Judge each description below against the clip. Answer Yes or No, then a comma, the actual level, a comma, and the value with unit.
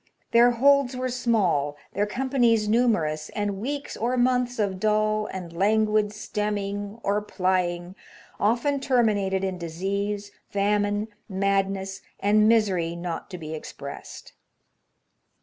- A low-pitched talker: No, high, 205 Hz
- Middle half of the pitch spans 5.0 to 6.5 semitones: No, average, 3.3 semitones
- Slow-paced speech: Yes, slow, 130 wpm